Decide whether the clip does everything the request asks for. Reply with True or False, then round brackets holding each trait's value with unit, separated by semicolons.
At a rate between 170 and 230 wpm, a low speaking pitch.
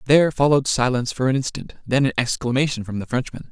True (205 wpm; 130 Hz)